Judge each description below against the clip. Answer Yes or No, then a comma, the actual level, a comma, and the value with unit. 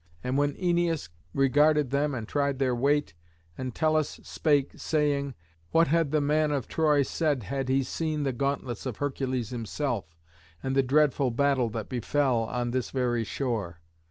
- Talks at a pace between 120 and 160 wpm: Yes, average, 155 wpm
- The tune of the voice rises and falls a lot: No, average, 3.1 semitones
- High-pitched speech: No, low, 135 Hz